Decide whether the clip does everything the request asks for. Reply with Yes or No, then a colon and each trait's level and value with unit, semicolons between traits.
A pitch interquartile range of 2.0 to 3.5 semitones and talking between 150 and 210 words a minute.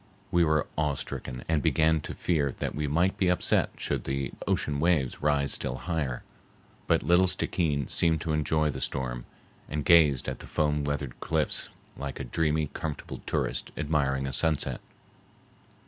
Yes: average, 2.7 semitones; average, 165 wpm